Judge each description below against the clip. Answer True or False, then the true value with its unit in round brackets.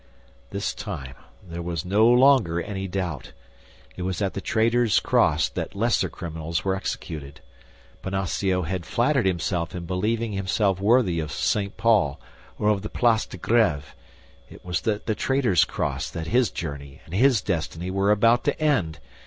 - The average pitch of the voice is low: True (95 Hz)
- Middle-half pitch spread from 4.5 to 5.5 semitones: True (4.8 semitones)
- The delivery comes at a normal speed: True (160 wpm)